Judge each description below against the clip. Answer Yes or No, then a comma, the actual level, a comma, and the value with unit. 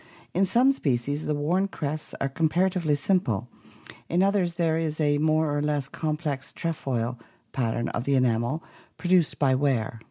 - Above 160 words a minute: No, average, 155 wpm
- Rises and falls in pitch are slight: No, average, 4.1 semitones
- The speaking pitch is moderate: Yes, medium, 150 Hz